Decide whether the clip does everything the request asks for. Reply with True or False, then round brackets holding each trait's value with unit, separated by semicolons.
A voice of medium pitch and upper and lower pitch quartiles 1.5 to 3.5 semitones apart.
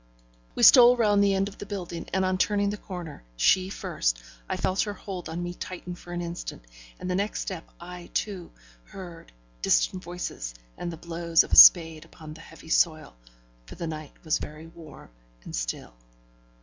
True (175 Hz; 2.8 semitones)